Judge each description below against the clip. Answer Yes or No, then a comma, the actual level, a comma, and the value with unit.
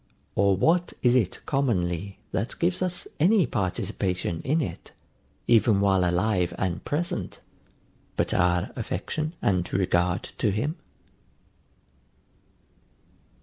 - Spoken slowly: Yes, slow, 105 wpm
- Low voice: Yes, low, 100 Hz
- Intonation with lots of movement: Yes, wide, 7.4 semitones